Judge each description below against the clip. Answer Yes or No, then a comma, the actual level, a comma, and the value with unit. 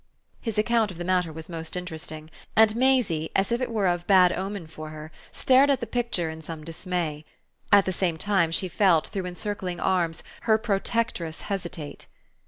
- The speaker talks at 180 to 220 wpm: Yes, average, 185 wpm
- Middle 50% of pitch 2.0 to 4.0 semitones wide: No, average, 4.4 semitones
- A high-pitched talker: No, medium, 180 Hz